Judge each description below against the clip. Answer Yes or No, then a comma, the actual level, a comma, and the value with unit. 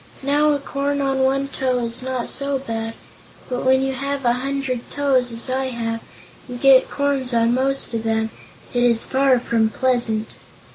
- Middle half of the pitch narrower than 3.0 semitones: Yes, narrow, 2.5 semitones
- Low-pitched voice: No, very high, 260 Hz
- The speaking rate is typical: Yes, average, 180 wpm